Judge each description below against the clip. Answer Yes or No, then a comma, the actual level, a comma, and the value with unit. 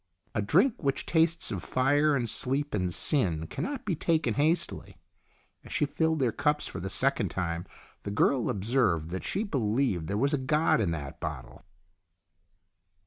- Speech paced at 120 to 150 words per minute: No, average, 170 wpm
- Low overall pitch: Yes, low, 130 Hz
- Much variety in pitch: Yes, wide, 7.7 semitones